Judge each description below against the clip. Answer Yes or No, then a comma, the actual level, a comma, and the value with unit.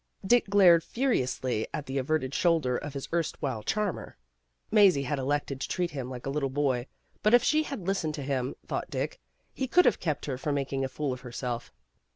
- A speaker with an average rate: No, fast, 210 wpm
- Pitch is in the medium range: Yes, medium, 145 Hz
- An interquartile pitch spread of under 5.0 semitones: No, wide, 5.6 semitones